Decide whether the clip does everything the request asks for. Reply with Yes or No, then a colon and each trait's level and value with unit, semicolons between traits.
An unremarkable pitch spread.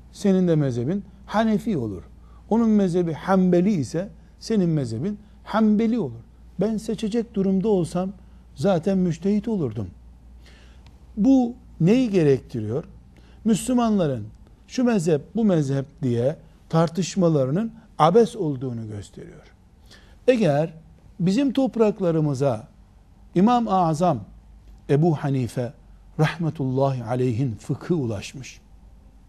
No: wide, 8.3 semitones